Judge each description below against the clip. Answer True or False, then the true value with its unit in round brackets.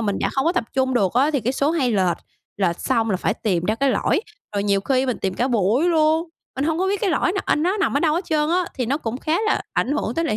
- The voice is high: True (270 Hz)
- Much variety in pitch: True (6.6 semitones)